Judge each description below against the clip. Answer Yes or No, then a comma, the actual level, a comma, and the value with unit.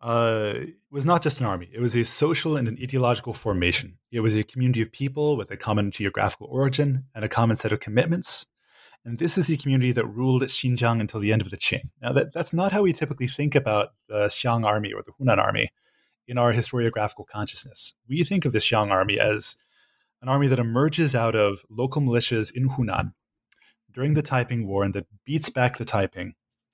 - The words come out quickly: Yes, fast, 210 wpm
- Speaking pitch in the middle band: No, low, 120 Hz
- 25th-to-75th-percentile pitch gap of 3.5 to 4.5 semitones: Yes, average, 4.0 semitones